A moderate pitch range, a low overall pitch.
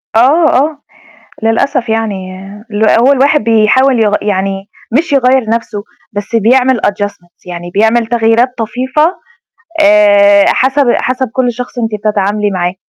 No: average, 4.1 semitones; high, 225 Hz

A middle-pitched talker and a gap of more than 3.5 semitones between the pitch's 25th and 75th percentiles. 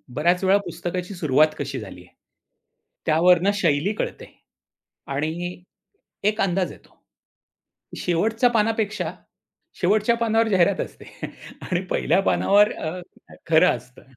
Yes: medium, 180 Hz; average, 4.8 semitones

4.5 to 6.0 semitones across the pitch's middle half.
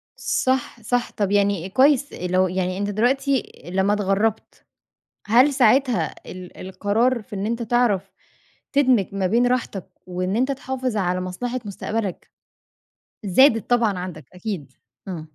Yes: average, 4.9 semitones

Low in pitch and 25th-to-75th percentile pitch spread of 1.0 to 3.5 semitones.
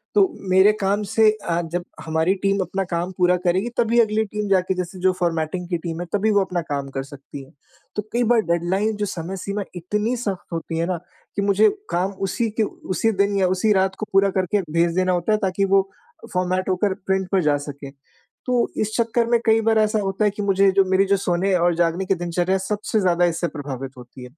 No: high, 190 Hz; average, 3.1 semitones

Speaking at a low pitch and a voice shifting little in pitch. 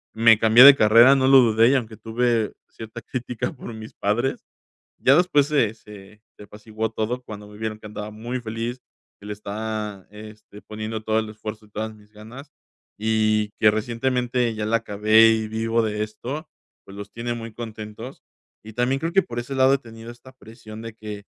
Yes: low, 110 Hz; narrow, 2.1 semitones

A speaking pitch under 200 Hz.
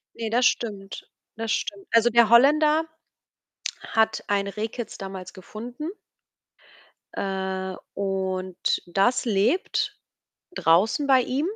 No: high, 215 Hz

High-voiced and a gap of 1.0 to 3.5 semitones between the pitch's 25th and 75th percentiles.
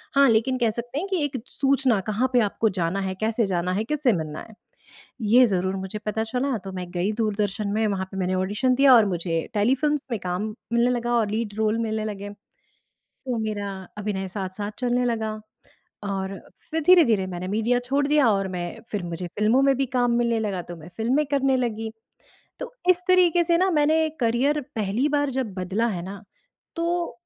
No: high, 225 Hz; average, 5.2 semitones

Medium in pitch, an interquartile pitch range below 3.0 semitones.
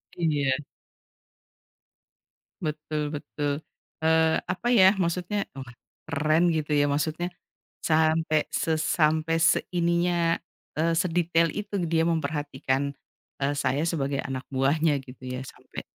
Yes: medium, 155 Hz; narrow, 2.4 semitones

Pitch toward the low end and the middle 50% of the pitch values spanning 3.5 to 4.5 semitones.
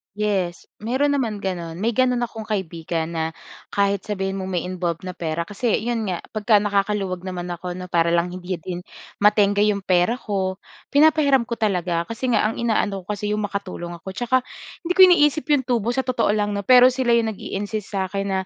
No: high, 200 Hz; average, 4.2 semitones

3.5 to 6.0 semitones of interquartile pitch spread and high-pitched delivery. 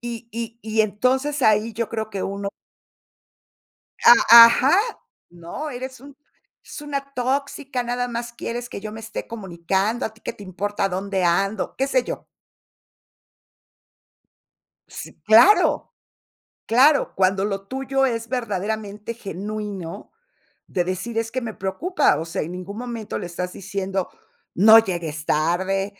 Yes: average, 3.8 semitones; high, 220 Hz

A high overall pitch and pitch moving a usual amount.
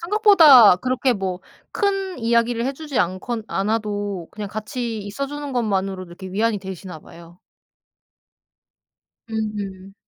Yes: high, 215 Hz; average, 4.9 semitones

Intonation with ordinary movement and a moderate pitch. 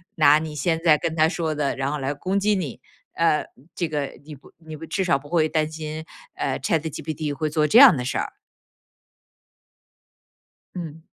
No: narrow, 1.8 semitones; medium, 155 Hz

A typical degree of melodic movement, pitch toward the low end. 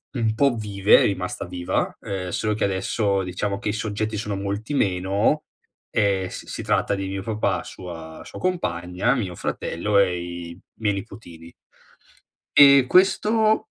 Yes: average, 3.3 semitones; low, 100 Hz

